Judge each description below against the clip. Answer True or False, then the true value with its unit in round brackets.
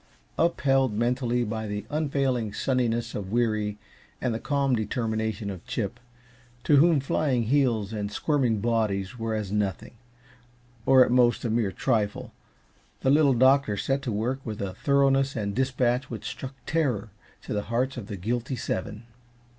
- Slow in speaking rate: False (155 wpm)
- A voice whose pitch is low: True (120 Hz)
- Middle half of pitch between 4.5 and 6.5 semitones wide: False (3.8 semitones)